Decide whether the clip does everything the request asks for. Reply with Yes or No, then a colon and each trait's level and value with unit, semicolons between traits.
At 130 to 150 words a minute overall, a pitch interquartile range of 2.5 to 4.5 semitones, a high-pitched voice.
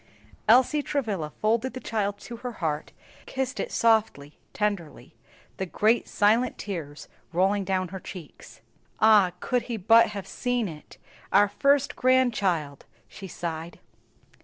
No: slow, 135 wpm; average, 5.0 semitones; high, 205 Hz